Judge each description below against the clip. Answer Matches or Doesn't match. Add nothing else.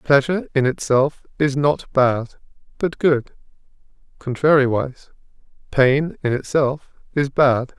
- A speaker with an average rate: Doesn't match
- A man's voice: Matches